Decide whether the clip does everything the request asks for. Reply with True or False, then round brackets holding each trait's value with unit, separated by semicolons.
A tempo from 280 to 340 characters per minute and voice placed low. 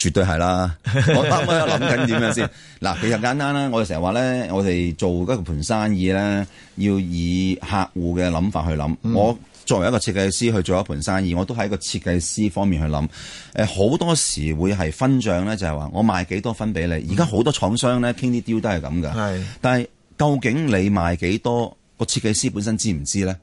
True (315 characters per minute; 100 Hz)